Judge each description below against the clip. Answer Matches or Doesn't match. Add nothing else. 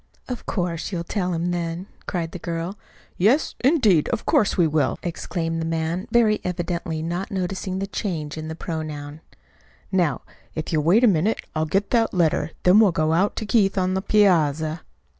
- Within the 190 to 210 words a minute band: Doesn't match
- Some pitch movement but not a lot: Matches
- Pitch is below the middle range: Doesn't match